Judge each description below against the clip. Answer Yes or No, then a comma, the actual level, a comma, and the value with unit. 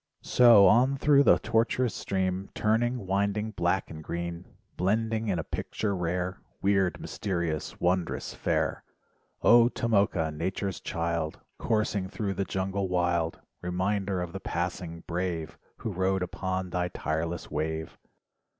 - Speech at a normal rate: No, slow, 130 wpm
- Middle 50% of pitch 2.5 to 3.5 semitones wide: Yes, average, 3.0 semitones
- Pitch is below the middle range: Yes, very low, 95 Hz